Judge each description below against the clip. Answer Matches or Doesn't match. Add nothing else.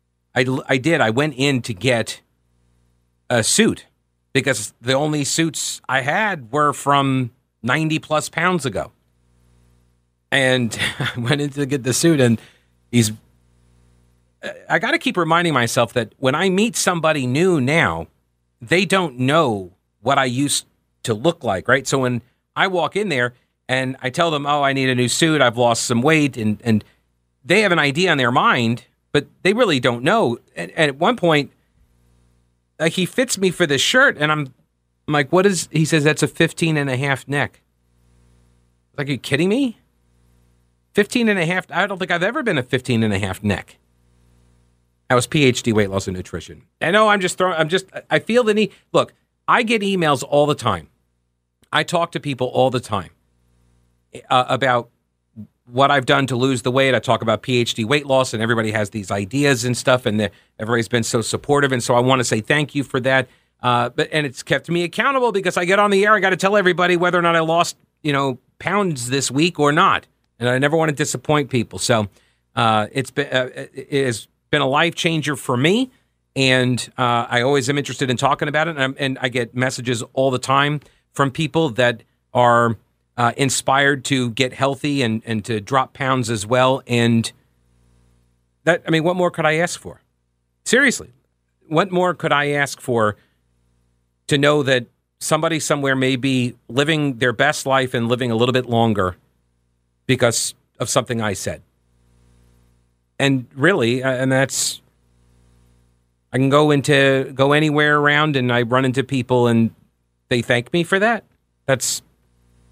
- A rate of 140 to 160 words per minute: Doesn't match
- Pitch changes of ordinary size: Doesn't match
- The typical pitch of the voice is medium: Doesn't match